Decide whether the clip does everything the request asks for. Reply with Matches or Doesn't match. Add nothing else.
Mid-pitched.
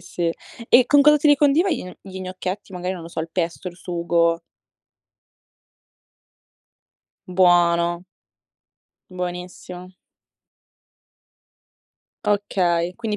Matches